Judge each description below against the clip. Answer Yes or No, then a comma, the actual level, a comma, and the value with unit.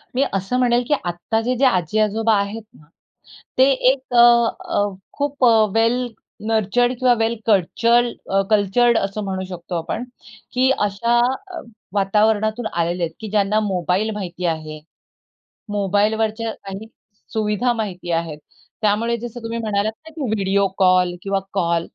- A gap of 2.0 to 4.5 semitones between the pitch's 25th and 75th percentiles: Yes, average, 3.4 semitones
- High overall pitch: Yes, high, 215 Hz